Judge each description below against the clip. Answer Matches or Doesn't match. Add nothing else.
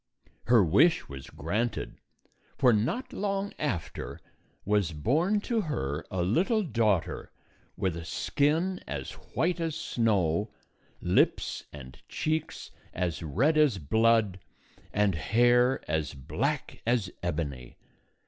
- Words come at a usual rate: Doesn't match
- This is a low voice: Matches